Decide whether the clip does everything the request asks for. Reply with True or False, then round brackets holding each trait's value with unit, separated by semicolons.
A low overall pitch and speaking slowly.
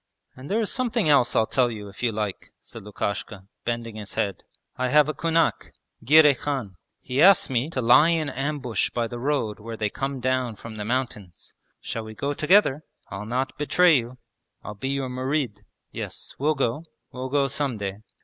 False (130 Hz; 190 wpm)